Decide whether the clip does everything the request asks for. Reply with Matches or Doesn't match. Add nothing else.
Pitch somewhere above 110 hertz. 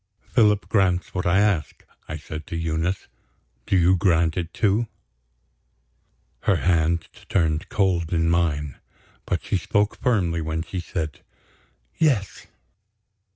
Doesn't match